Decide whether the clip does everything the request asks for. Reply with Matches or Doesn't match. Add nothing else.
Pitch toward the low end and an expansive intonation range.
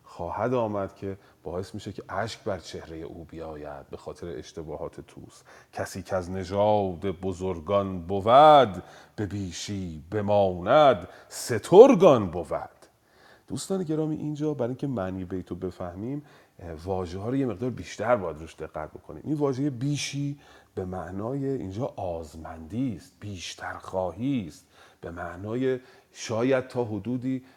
Matches